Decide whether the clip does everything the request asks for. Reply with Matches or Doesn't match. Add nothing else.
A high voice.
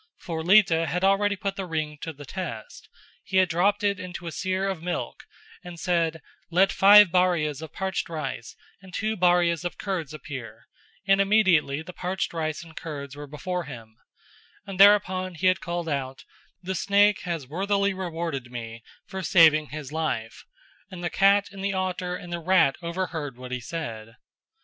Doesn't match